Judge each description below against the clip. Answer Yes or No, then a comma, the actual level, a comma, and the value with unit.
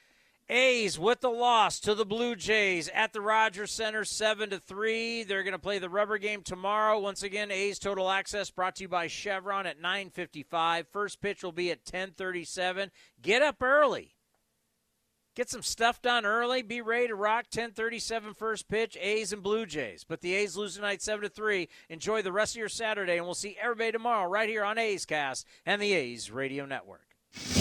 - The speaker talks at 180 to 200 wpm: Yes, average, 185 wpm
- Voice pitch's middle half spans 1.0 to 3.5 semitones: Yes, average, 3.0 semitones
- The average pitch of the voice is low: No, high, 205 Hz